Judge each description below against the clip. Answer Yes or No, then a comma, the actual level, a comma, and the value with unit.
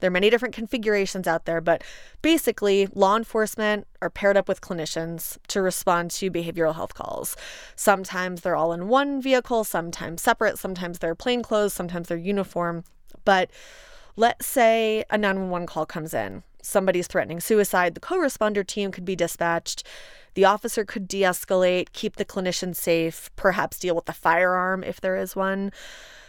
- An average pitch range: Yes, average, 3.8 semitones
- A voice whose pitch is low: No, high, 190 Hz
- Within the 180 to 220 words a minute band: No, average, 160 wpm